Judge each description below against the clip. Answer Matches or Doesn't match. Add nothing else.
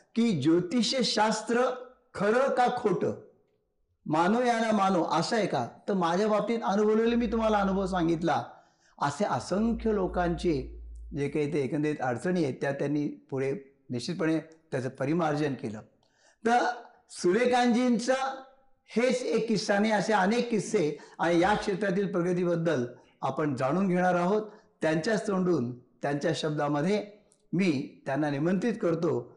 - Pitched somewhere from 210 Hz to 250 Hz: Doesn't match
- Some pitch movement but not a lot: Doesn't match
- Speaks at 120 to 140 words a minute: Matches